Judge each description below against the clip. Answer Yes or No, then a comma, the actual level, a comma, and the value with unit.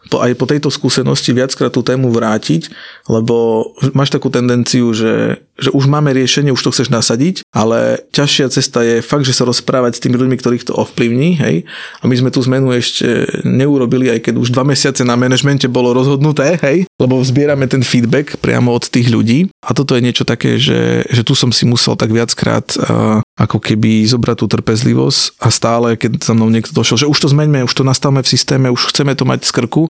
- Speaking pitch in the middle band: No, low, 125 Hz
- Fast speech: Yes, fast, 200 wpm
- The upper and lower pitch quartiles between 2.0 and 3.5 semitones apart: Yes, average, 2.7 semitones